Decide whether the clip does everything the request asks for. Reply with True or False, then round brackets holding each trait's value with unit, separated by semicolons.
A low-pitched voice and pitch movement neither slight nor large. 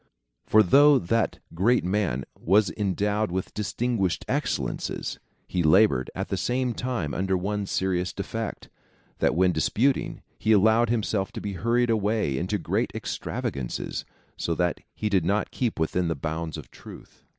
True (100 Hz; 4.0 semitones)